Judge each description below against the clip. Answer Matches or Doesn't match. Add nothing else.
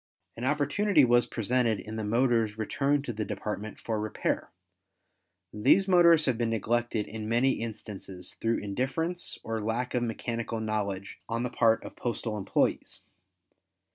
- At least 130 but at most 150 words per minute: Matches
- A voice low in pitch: Matches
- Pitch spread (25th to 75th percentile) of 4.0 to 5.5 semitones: Doesn't match